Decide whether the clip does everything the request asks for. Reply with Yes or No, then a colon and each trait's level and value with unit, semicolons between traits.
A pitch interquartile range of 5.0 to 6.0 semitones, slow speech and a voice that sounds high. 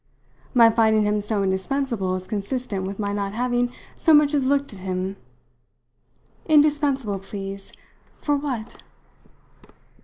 Yes: wide, 5.6 semitones; slow, 125 wpm; high, 220 Hz